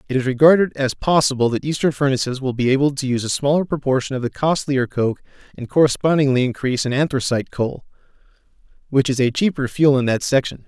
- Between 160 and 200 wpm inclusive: Yes, average, 190 wpm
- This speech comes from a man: Yes, male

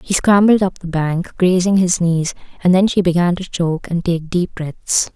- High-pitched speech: No, medium, 175 Hz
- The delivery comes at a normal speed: No, fast, 210 wpm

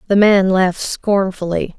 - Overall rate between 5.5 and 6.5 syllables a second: No, 4.4 syllables/s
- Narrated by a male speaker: No, female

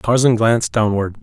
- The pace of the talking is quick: No, average, 145 wpm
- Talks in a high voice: No, low, 110 Hz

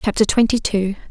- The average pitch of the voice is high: Yes, high, 210 Hz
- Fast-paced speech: No, average, 165 wpm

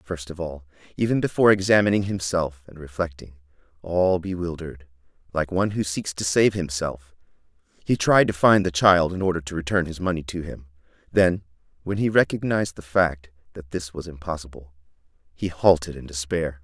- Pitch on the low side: Yes, very low, 85 Hz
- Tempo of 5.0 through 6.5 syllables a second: Yes, 5.5 syllables/s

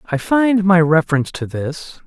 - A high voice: No, medium, 170 Hz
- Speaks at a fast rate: No, average, 175 wpm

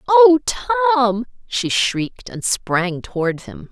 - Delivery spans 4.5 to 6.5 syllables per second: No, 3.6 syllables/s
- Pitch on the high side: Yes, high, 245 Hz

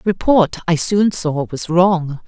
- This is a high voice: No, medium, 175 Hz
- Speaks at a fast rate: No, average, 160 wpm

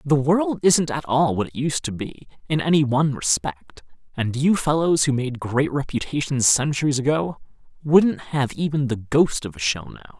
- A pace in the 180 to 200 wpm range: Yes, average, 190 wpm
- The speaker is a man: Yes, male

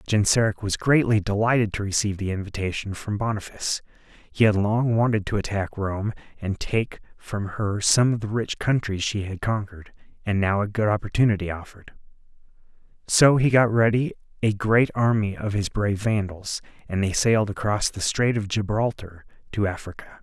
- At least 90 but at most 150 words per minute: No, average, 165 wpm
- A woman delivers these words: No, male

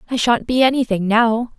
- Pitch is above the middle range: Yes, high, 235 Hz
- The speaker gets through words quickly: No, average, 190 wpm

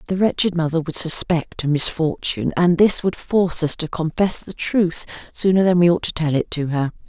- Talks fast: Yes, fast, 210 wpm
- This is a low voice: No, medium, 170 Hz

